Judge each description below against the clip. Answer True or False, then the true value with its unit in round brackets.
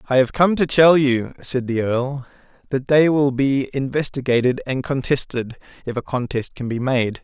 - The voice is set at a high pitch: False (130 Hz)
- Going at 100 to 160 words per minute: False (180 wpm)